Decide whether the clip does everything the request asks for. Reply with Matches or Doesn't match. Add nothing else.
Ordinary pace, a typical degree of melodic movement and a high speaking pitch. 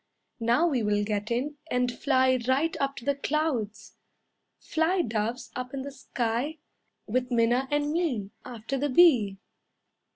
Matches